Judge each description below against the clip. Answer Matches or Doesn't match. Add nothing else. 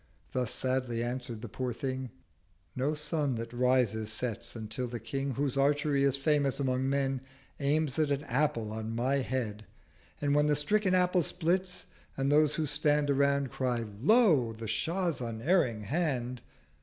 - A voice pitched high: Doesn't match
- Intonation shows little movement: Doesn't match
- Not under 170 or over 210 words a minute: Doesn't match